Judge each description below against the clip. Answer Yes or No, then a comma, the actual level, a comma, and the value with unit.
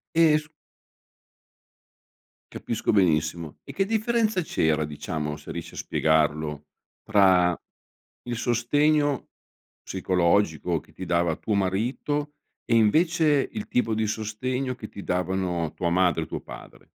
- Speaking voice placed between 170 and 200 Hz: No, low, 100 Hz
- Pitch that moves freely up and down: Yes, wide, 8.1 semitones